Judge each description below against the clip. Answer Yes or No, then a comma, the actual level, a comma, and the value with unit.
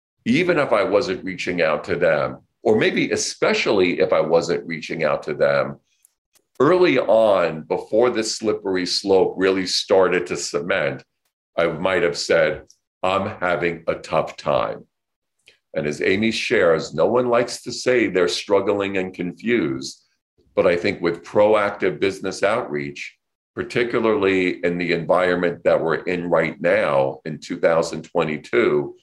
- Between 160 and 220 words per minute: No, average, 140 wpm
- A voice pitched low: Yes, very low, 95 Hz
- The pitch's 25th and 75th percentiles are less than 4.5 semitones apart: Yes, average, 3.7 semitones